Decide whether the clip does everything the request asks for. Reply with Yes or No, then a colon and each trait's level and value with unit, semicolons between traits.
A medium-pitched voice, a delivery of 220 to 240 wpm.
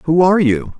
Yes: medium, 160 Hz; fast, 225 wpm